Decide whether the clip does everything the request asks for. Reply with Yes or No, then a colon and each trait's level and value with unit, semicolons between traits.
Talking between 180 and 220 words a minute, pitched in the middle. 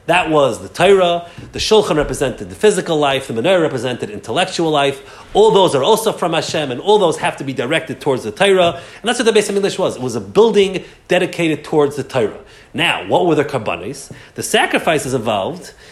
Yes: fast, 205 wpm; medium, 175 Hz